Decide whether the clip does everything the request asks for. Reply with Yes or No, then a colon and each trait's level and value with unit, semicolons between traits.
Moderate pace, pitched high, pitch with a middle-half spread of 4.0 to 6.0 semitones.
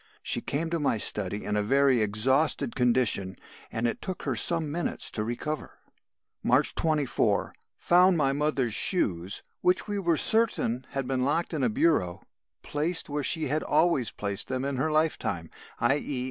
No: average, 170 wpm; low, 135 Hz; wide, 5.6 semitones